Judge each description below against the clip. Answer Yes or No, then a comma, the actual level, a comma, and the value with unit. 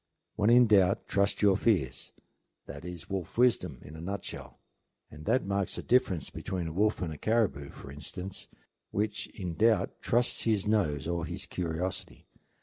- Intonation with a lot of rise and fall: No, average, 4.7 semitones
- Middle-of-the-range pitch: No, very low, 95 Hz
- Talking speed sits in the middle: Yes, average, 165 wpm